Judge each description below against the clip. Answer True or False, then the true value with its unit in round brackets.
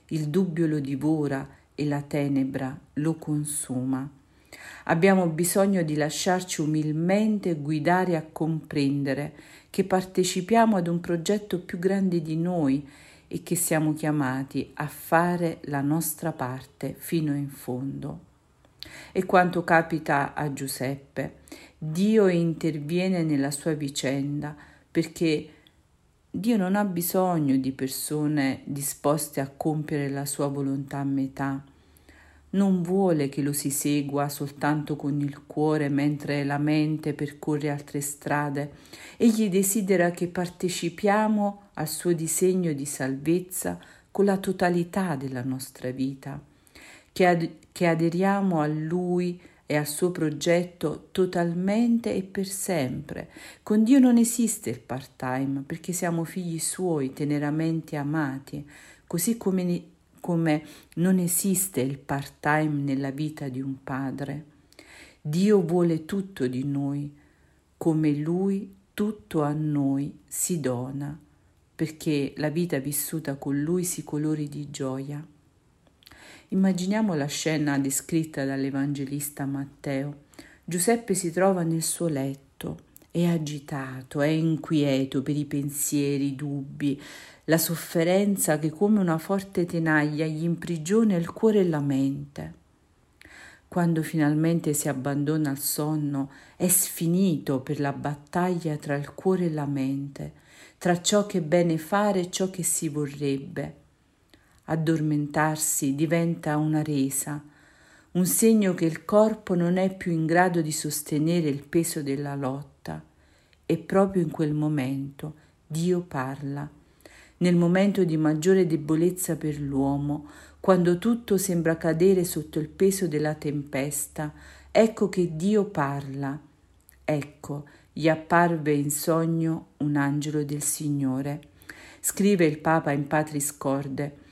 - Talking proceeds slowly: False (125 wpm)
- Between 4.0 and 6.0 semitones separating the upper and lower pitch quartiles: False (3.6 semitones)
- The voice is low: False (155 Hz)